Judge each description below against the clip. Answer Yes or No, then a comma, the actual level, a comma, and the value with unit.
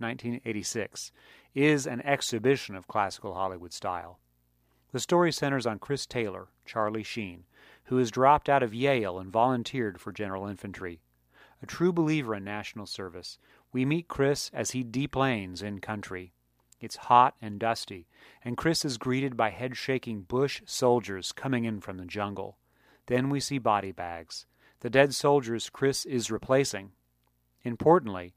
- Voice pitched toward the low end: Yes, low, 115 Hz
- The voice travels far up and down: Yes, wide, 5.8 semitones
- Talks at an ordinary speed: Yes, average, 150 wpm